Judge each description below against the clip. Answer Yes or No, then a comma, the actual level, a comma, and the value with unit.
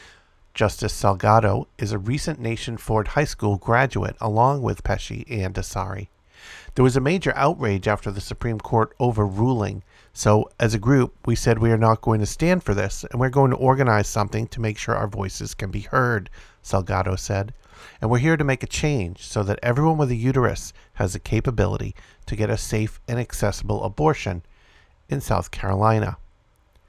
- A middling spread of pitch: Yes, average, 3.7 semitones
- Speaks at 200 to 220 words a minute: No, average, 180 wpm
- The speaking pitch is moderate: No, low, 110 Hz